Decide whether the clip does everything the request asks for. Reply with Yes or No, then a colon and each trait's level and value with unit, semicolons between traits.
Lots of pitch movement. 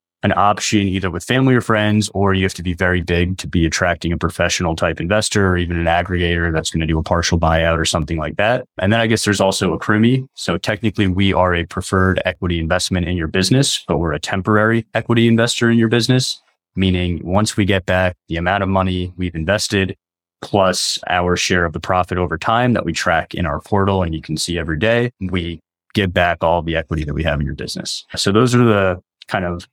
No: average, 3.4 semitones